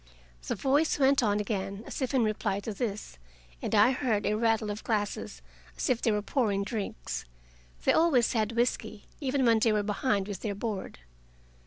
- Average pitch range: Yes, average, 3.3 semitones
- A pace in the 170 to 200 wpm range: Yes, average, 185 wpm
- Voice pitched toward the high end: Yes, high, 215 Hz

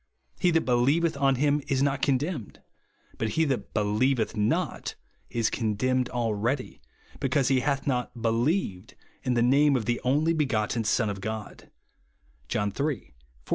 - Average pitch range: Yes, average, 4.1 semitones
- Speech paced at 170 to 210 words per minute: No, average, 160 wpm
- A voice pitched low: Yes, low, 125 Hz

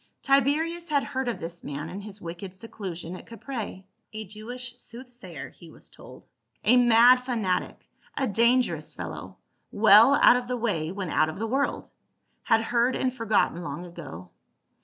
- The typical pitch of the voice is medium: No, high, 225 Hz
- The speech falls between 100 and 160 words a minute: No, average, 175 wpm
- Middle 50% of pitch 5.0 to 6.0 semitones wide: Yes, wide, 5.6 semitones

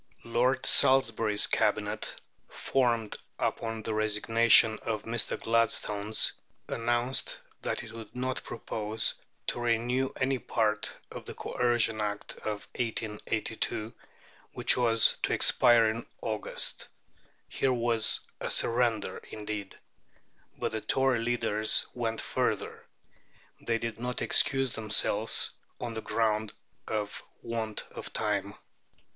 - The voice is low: Yes, low, 115 Hz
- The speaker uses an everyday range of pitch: No, narrow, 1.8 semitones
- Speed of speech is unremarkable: No, slow, 115 wpm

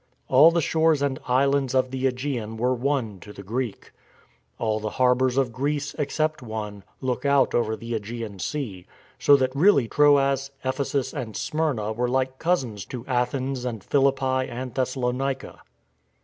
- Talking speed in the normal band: Yes, average, 155 wpm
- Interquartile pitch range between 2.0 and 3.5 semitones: Yes, average, 2.9 semitones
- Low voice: Yes, low, 130 Hz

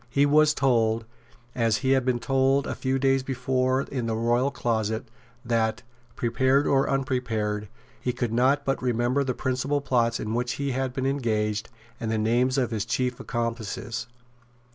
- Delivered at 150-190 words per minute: Yes, average, 165 wpm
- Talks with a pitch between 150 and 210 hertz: No, low, 125 Hz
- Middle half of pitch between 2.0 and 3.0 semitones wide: Yes, narrow, 2.6 semitones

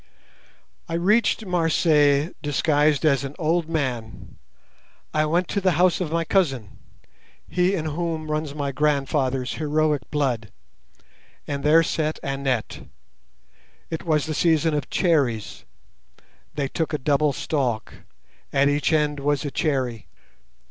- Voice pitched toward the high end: No, medium, 150 Hz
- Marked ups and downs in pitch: No, average, 2.7 semitones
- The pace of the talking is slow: Yes, slow, 125 wpm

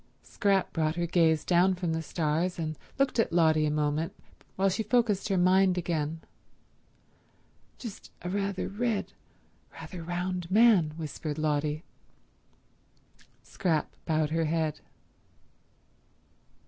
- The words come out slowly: Yes, slow, 120 wpm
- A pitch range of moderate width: Yes, average, 3.5 semitones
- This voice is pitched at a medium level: Yes, medium, 170 Hz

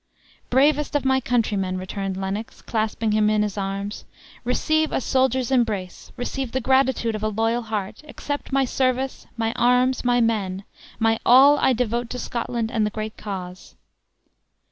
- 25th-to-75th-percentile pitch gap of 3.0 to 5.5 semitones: Yes, average, 3.6 semitones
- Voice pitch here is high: Yes, high, 230 Hz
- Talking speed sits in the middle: Yes, average, 160 wpm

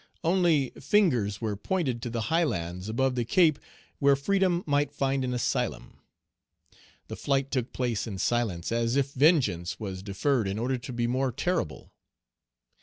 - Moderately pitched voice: No, low, 130 Hz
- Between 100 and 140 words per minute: No, average, 160 wpm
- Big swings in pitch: No, average, 4.2 semitones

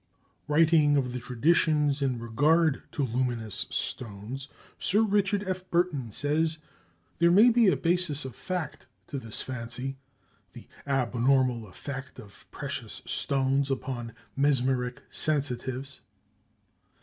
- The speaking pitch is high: No, low, 135 Hz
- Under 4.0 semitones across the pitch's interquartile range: No, average, 4.3 semitones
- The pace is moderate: No, slow, 115 wpm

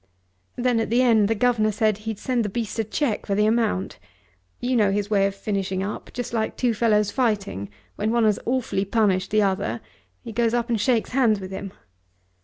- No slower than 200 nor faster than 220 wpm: Yes, fast, 205 wpm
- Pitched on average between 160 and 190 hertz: No, high, 215 Hz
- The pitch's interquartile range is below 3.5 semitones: Yes, average, 2.8 semitones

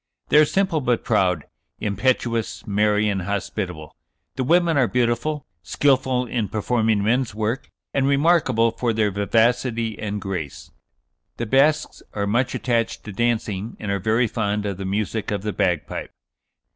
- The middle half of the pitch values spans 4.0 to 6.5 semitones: No, average, 3.6 semitones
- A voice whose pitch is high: No, low, 110 Hz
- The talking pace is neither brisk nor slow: Yes, average, 150 wpm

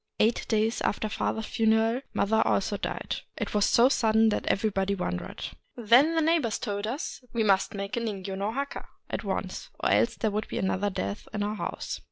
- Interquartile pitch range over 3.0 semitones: No, narrow, 2.5 semitones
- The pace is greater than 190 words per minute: Yes, fast, 205 wpm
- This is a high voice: Yes, high, 215 Hz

